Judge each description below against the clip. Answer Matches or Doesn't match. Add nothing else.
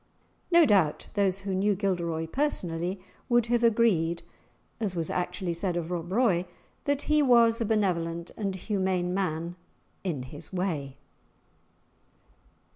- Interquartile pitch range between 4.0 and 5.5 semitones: Matches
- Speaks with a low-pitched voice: Doesn't match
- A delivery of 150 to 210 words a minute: Doesn't match